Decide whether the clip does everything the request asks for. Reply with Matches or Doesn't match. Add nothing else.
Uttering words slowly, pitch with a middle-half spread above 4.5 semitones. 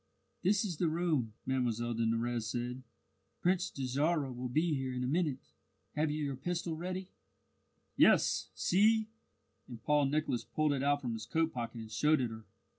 Doesn't match